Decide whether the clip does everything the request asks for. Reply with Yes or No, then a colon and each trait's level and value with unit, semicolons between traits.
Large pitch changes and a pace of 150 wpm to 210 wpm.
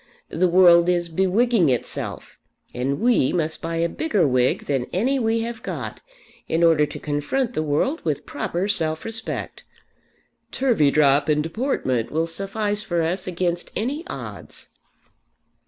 No: wide, 6.3 semitones; average, 140 wpm